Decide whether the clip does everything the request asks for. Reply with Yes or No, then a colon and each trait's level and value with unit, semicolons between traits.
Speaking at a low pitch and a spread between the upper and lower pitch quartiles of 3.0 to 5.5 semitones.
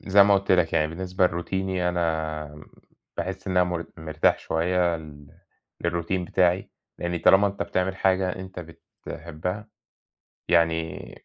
No: very low, 90 Hz; narrow, 2.4 semitones